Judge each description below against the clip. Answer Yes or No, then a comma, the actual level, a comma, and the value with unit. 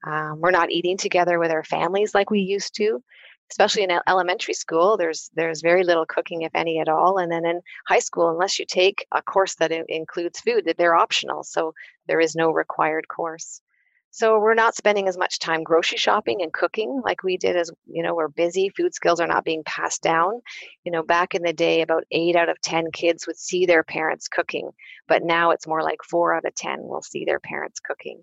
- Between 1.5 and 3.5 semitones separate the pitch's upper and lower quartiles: Yes, average, 3.2 semitones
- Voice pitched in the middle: Yes, medium, 170 Hz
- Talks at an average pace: No, fast, 220 wpm